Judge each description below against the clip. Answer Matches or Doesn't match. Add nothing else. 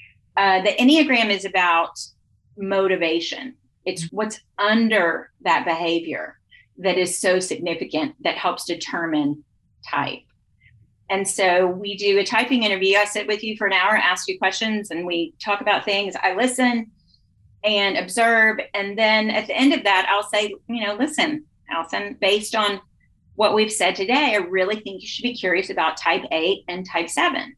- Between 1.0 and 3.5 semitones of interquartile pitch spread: Doesn't match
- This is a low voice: Doesn't match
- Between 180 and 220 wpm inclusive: Doesn't match